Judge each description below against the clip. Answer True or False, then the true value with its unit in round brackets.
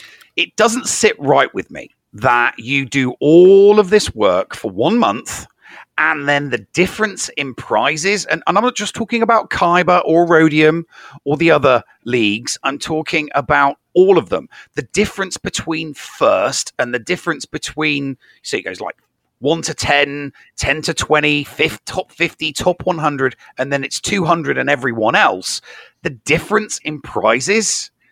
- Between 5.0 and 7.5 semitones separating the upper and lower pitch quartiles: True (5.4 semitones)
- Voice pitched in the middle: True (155 Hz)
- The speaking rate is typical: True (160 wpm)